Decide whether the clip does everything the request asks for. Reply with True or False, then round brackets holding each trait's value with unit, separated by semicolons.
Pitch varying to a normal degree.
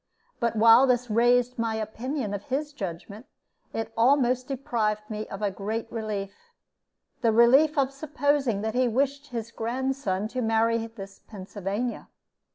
True (3.3 semitones)